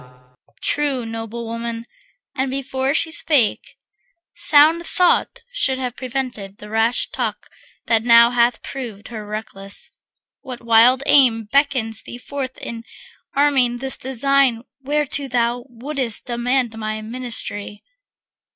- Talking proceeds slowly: Yes, slow, 120 wpm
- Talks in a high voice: Yes, high, 245 Hz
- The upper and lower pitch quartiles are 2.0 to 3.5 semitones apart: Yes, average, 3.2 semitones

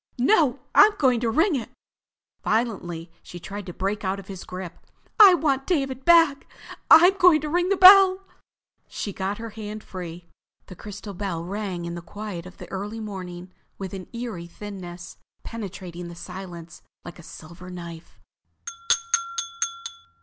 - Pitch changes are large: Yes, wide, 6.6 semitones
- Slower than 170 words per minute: Yes, average, 155 wpm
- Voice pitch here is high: Yes, high, 200 Hz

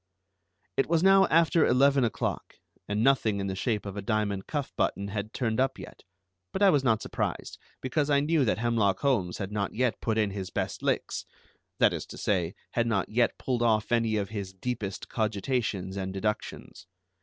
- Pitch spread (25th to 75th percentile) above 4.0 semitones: Yes, average, 4.6 semitones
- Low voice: Yes, low, 110 Hz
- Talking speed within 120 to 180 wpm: No, average, 190 wpm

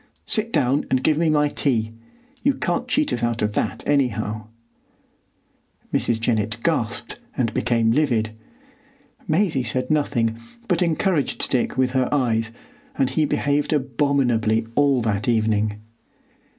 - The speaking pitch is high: No, low, 125 Hz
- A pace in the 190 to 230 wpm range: No, slow, 135 wpm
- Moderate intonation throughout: Yes, average, 4.7 semitones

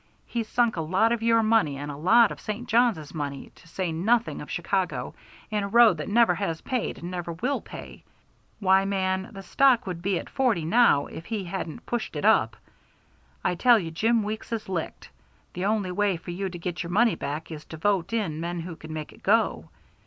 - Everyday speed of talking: No, fast, 215 wpm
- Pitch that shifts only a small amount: No, average, 5.3 semitones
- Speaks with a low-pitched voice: No, high, 190 Hz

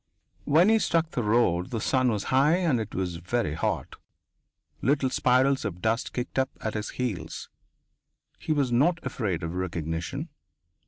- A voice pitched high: No, low, 120 Hz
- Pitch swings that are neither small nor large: No, wide, 6.9 semitones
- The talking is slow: No, average, 160 wpm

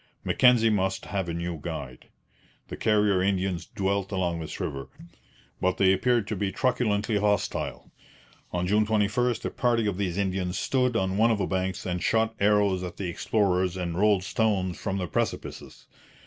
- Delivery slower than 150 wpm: No, average, 170 wpm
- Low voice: Yes, very low, 95 Hz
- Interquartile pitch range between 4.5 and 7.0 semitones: No, average, 2.7 semitones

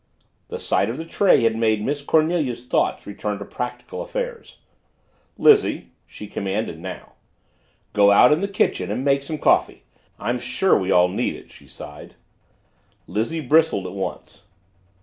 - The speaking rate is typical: Yes, average, 155 wpm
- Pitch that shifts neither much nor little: No, wide, 7.7 semitones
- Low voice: Yes, low, 125 Hz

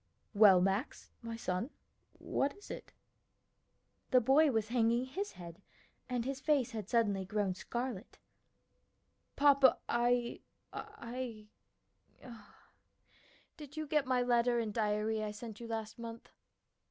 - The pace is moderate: No, slow, 125 wpm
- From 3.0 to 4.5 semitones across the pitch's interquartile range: Yes, average, 3.4 semitones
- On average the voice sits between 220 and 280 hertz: Yes, high, 235 Hz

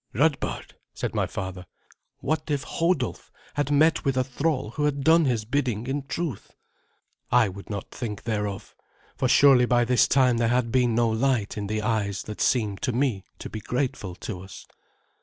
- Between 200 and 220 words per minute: No, average, 180 wpm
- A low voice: Yes, low, 125 Hz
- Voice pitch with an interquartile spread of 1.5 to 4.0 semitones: No, average, 4.5 semitones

